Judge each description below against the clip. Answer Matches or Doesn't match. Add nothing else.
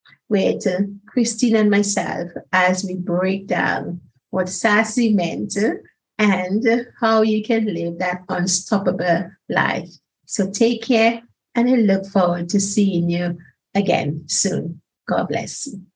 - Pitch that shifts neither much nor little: Matches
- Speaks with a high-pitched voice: Matches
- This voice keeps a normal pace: Doesn't match